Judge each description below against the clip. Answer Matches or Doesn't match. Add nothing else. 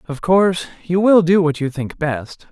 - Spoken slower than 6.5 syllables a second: Matches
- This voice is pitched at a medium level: Matches